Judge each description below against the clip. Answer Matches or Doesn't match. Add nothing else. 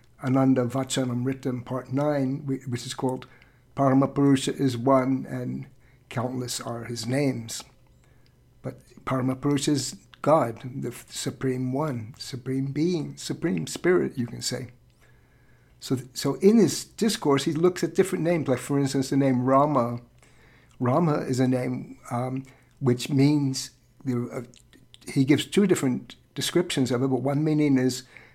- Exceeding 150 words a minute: Doesn't match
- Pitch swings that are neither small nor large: Doesn't match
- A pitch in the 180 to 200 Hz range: Doesn't match